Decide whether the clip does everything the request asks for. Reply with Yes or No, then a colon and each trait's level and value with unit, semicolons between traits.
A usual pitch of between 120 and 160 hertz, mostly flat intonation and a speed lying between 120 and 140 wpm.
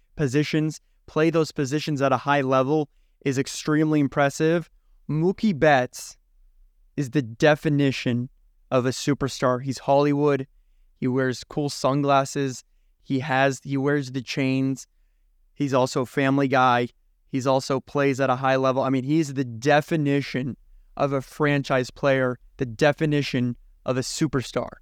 Yes: low, 135 Hz; narrow, 2.3 semitones; slow, 135 wpm